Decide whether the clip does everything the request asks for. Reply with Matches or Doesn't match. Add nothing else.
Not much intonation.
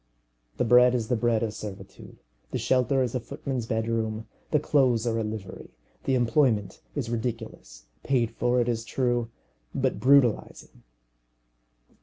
Matches